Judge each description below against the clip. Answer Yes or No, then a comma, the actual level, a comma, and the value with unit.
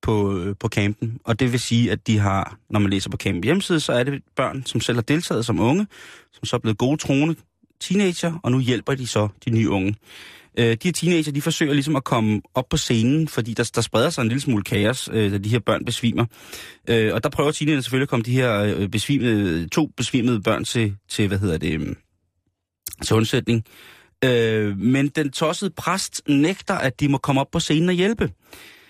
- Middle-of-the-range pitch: No, low, 120 Hz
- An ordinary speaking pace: Yes, average, 215 wpm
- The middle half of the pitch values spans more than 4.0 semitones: Yes, average, 5.0 semitones